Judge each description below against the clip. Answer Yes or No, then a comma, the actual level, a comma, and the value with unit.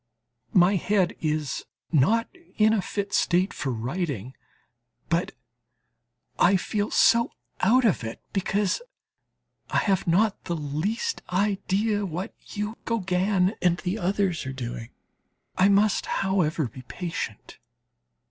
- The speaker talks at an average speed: No, slow, 120 wpm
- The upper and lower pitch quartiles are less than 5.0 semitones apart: Yes, average, 4.1 semitones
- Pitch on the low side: No, medium, 185 Hz